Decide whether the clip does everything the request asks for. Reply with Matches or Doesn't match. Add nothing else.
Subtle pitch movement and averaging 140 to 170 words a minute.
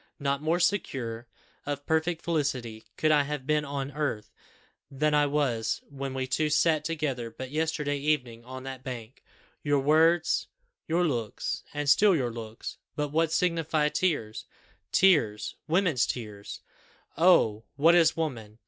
Doesn't match